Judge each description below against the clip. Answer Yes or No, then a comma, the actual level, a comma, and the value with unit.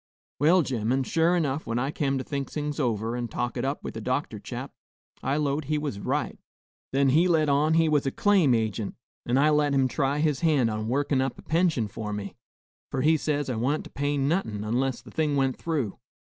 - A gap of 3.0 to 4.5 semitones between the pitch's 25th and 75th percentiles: Yes, average, 3.8 semitones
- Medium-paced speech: No, fast, 220 wpm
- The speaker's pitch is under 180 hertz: Yes, medium, 140 Hz